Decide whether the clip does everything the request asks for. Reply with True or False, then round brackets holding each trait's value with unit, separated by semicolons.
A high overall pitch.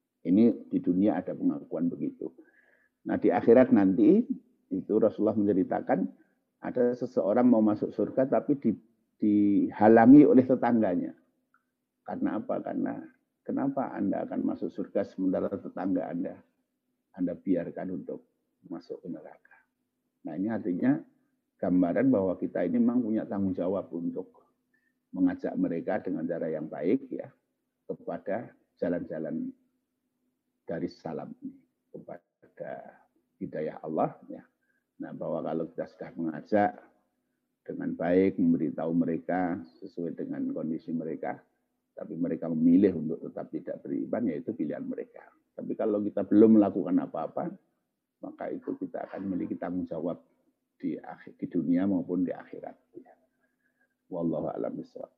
True (260 Hz)